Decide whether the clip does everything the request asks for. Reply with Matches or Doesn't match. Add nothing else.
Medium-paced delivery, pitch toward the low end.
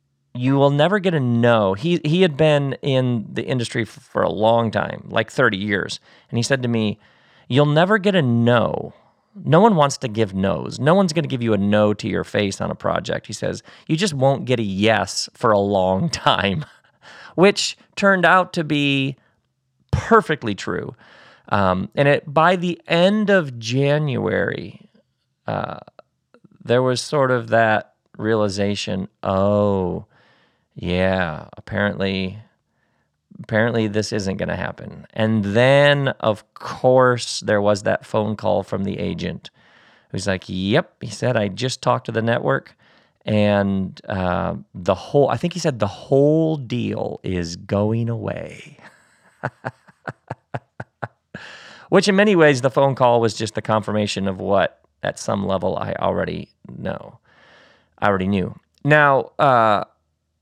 Matches